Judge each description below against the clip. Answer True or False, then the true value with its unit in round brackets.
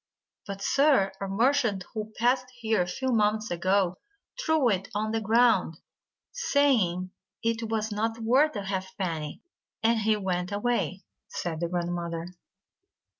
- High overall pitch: True (210 Hz)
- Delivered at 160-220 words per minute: False (140 wpm)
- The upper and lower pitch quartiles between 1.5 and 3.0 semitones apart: False (4.1 semitones)